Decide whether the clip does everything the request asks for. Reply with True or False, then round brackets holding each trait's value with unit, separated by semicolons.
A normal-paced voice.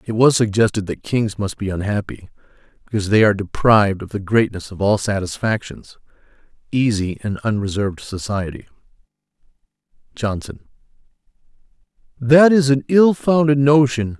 False (125 wpm)